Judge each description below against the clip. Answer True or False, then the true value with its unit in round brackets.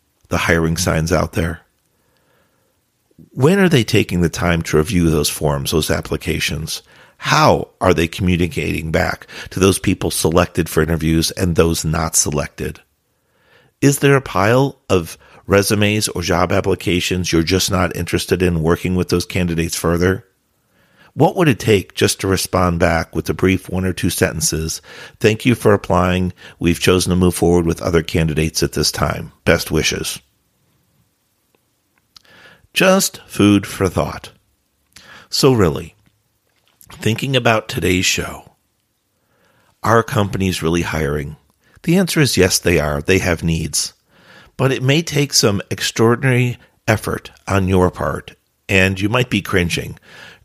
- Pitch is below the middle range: True (90 Hz)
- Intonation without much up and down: False (3.7 semitones)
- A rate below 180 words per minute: True (145 wpm)